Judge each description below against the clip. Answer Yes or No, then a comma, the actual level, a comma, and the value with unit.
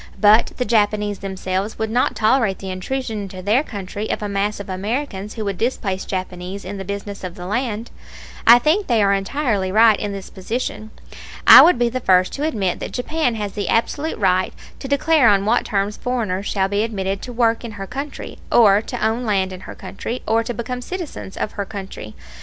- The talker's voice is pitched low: No, high, 210 Hz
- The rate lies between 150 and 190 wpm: No, fast, 205 wpm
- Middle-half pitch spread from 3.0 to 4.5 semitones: Yes, average, 3.6 semitones